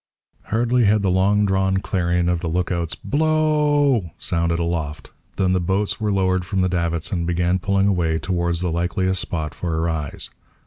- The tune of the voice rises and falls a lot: No, average, 2.7 semitones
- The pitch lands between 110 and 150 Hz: No, very low, 90 Hz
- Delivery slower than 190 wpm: No, average, 195 wpm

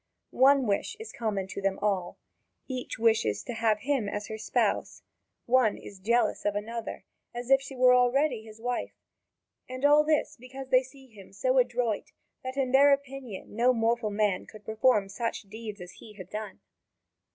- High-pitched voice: Yes, high, 235 Hz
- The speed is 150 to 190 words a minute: Yes, average, 180 wpm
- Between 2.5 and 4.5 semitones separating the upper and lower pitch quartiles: Yes, average, 3.7 semitones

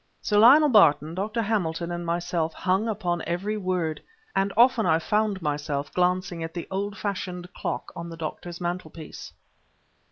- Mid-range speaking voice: Yes, medium, 180 Hz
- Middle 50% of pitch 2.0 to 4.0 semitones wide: Yes, average, 3.6 semitones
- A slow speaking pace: No, average, 160 wpm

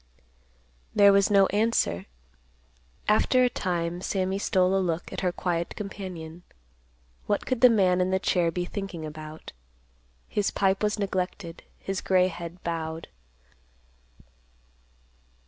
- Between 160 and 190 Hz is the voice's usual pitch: Yes, medium, 185 Hz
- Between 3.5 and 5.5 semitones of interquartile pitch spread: No, average, 2.8 semitones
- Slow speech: Yes, slow, 130 wpm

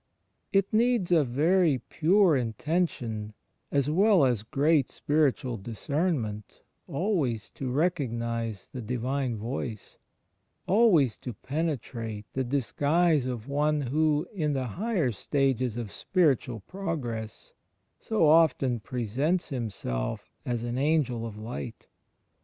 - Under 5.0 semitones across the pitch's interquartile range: No, wide, 5.4 semitones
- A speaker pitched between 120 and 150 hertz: Yes, low, 135 Hz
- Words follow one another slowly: Yes, slow, 110 wpm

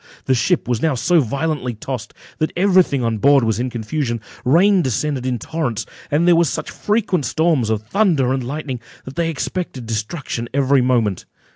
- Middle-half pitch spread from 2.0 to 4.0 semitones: No, wide, 5.4 semitones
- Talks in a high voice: No, low, 135 Hz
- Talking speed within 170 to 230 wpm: Yes, average, 180 wpm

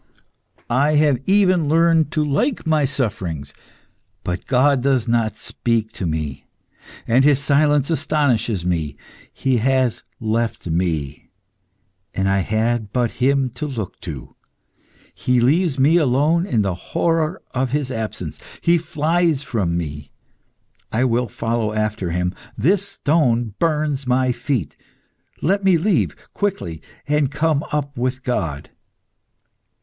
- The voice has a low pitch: Yes, low, 130 Hz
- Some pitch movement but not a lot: No, wide, 5.8 semitones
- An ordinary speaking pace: No, slow, 130 wpm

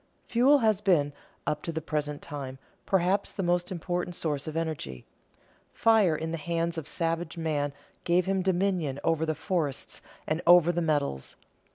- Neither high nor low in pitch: Yes, medium, 165 Hz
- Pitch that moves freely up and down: No, average, 2.9 semitones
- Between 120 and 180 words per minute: Yes, average, 165 wpm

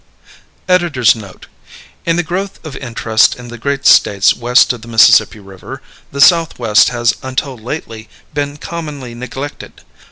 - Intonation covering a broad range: No, average, 4.4 semitones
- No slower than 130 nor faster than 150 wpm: Yes, average, 140 wpm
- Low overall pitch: Yes, low, 125 Hz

